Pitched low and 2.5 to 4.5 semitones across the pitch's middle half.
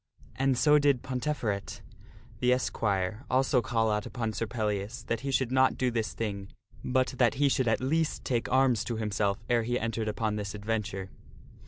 Yes: low, 115 Hz; average, 3.5 semitones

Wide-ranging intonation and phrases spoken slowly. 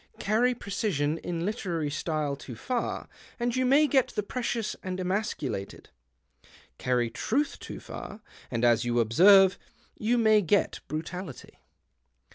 Yes: wide, 7.4 semitones; slow, 130 wpm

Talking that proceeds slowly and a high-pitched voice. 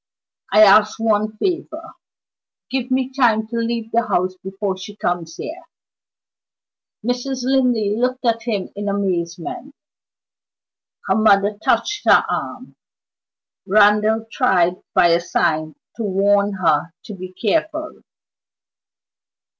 Yes: slow, 115 wpm; high, 215 Hz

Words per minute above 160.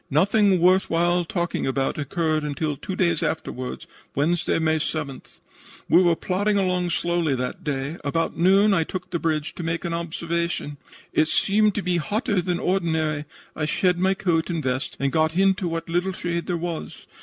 Yes: average, 180 wpm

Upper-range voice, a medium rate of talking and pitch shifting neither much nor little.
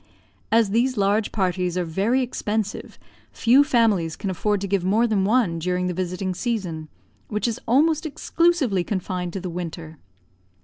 Yes: high, 200 Hz; average, 160 wpm; average, 4.3 semitones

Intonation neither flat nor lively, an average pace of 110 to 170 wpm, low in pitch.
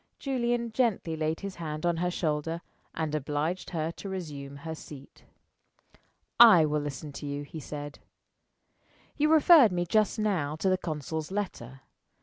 No: average, 4.8 semitones; average, 150 wpm; medium, 160 Hz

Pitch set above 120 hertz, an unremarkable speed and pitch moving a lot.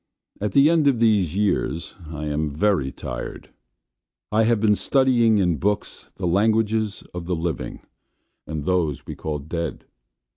No: very low, 95 Hz; average, 150 wpm; wide, 5.7 semitones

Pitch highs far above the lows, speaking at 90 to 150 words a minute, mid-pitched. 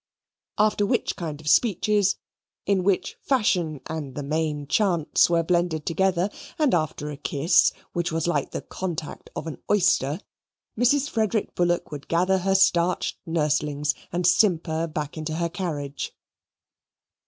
No: average, 3.8 semitones; average, 140 wpm; medium, 170 Hz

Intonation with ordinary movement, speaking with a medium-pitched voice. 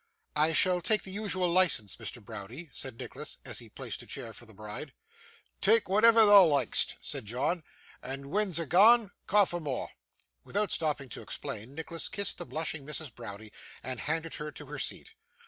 No: wide, 7.1 semitones; medium, 160 Hz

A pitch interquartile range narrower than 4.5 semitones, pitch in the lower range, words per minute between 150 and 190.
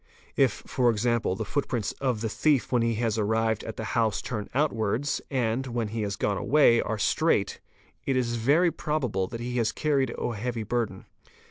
Yes: average, 2.7 semitones; low, 115 Hz; average, 180 wpm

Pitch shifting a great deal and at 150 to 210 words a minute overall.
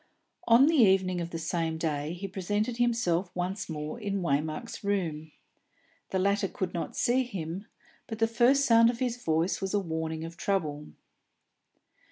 Yes: wide, 5.7 semitones; average, 165 wpm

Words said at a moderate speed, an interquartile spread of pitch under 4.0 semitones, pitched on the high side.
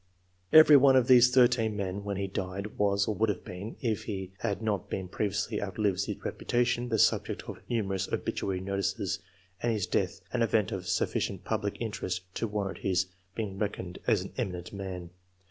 No: average, 185 wpm; average, 2.9 semitones; low, 100 Hz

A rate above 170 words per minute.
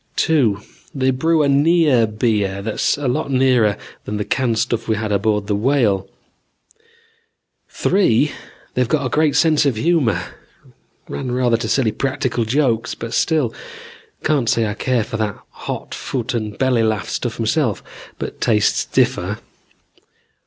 No: average, 145 wpm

